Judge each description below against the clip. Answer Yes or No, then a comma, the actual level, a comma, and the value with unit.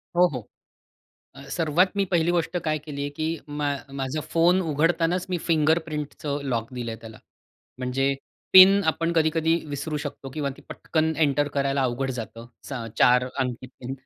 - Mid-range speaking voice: Yes, medium, 150 Hz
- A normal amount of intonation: Yes, average, 3.7 semitones